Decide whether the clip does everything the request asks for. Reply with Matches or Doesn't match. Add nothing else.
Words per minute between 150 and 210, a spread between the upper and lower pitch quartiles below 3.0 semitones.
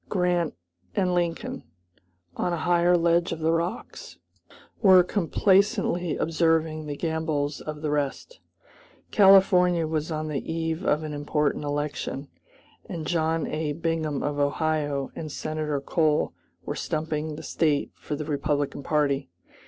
Doesn't match